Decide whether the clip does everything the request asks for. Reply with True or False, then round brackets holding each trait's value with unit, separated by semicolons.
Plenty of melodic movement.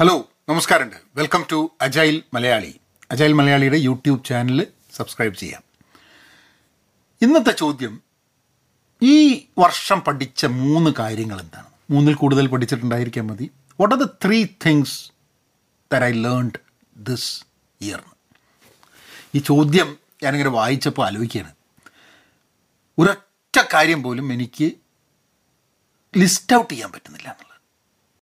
False (4.2 semitones)